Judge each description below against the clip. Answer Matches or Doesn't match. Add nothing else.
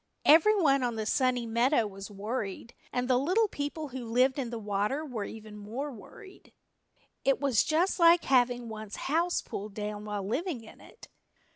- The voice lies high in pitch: Matches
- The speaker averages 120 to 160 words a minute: Doesn't match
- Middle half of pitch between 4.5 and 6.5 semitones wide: Matches